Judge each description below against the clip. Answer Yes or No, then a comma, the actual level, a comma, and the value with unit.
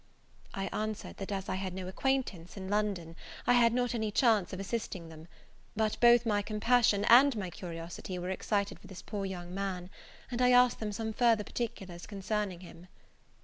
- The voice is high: Yes, high, 205 Hz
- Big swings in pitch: No, average, 3.7 semitones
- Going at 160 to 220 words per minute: Yes, average, 185 wpm